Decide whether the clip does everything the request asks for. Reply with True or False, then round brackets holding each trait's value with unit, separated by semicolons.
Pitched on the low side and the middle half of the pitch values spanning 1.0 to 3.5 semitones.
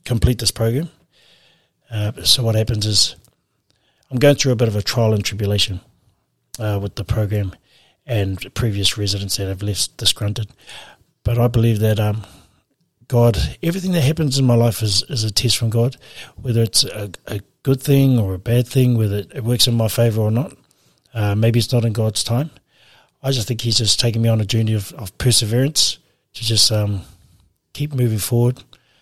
True (115 Hz; 3.0 semitones)